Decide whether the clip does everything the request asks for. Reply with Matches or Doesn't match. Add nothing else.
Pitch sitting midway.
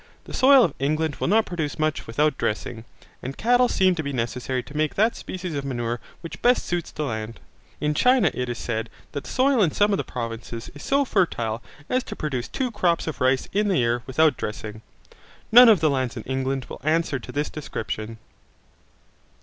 Matches